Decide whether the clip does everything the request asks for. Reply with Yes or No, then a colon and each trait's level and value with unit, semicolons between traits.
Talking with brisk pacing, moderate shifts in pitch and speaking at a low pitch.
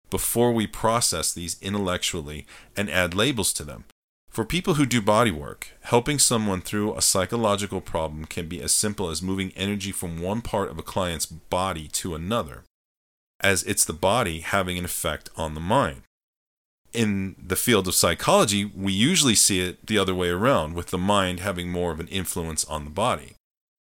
No: average, 180 wpm; average, 3.2 semitones; very low, 95 Hz